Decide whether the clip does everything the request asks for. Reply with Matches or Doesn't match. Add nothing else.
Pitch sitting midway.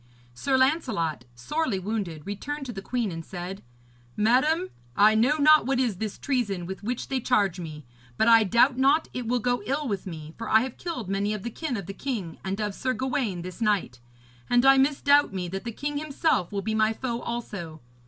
Doesn't match